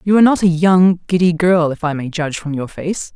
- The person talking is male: No, female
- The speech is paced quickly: Yes, fast, 265 wpm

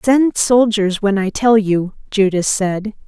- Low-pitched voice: No, high, 210 Hz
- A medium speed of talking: Yes, average, 155 wpm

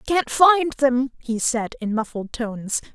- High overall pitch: Yes, very high, 255 Hz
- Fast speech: No, average, 185 wpm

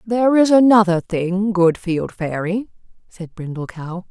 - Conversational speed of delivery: Yes, average, 145 wpm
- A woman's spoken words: Yes, female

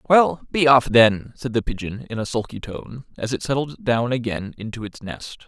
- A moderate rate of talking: No, fast, 210 wpm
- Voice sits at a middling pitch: No, low, 120 Hz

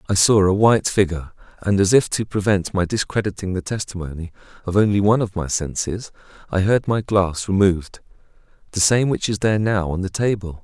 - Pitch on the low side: Yes, low, 100 Hz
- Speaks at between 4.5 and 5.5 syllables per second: No, 5.9 syllables/s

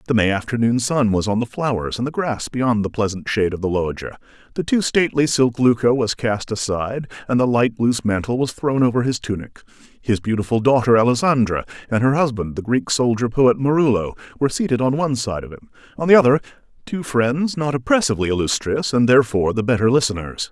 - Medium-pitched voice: No, low, 120 Hz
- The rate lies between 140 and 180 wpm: No, average, 200 wpm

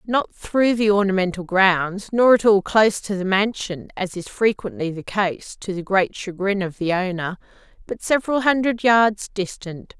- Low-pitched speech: No, high, 200 Hz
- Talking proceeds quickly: No, average, 160 wpm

